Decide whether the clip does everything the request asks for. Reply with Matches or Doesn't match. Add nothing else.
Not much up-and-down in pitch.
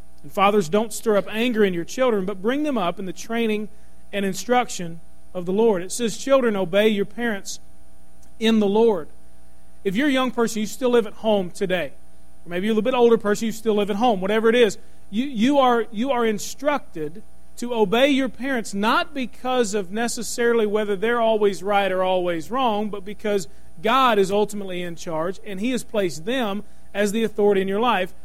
Doesn't match